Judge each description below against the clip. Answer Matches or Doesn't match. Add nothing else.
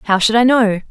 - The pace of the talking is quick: Matches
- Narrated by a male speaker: Doesn't match